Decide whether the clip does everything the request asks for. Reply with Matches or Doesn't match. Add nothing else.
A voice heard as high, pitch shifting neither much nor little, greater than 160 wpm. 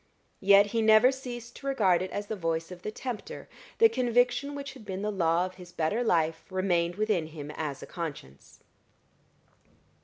Doesn't match